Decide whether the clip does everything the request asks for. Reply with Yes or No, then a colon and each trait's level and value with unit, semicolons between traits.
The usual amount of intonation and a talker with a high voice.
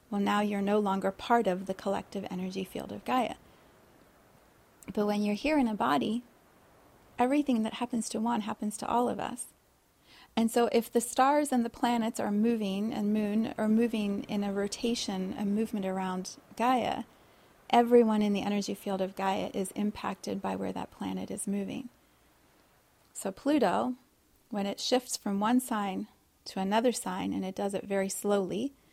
Yes: average, 3.2 semitones; high, 210 Hz